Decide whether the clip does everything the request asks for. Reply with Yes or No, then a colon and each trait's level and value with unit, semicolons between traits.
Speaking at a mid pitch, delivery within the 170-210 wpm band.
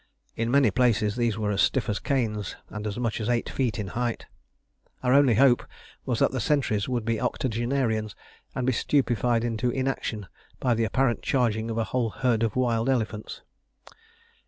No: low, 115 Hz; average, 180 wpm